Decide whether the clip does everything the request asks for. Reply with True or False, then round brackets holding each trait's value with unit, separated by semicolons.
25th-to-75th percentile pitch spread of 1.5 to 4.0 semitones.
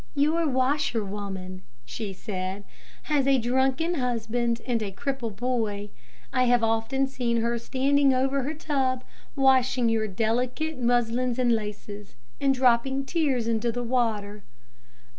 True (3.2 semitones)